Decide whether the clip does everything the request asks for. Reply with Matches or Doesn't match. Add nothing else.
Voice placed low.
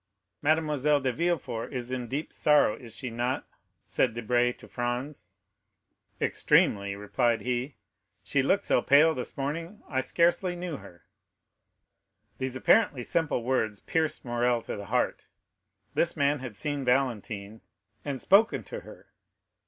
Matches